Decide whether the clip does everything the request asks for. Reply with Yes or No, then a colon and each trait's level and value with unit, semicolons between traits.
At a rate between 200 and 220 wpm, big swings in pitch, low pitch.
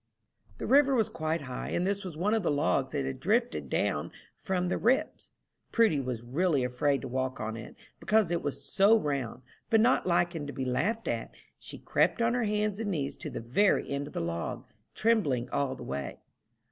No: fast, 205 wpm; wide, 8.1 semitones; medium, 160 Hz